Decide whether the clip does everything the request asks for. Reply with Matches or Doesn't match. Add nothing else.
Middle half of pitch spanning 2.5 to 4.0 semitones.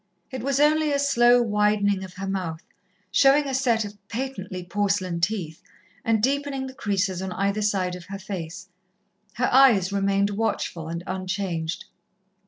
Doesn't match